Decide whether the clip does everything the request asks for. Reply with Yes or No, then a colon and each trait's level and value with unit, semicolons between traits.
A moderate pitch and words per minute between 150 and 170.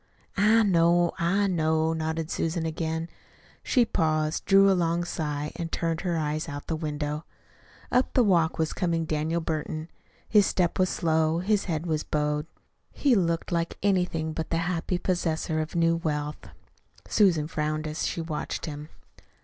Yes: medium, 165 Hz; average, 165 wpm